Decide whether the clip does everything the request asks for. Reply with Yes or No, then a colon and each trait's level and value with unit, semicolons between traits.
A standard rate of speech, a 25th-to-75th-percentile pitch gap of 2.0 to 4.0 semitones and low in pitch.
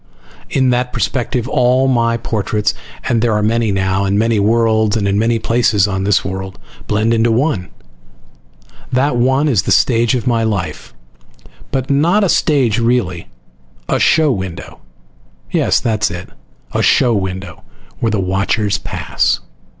Yes: average, 155 wpm; average, 3.7 semitones; low, 115 Hz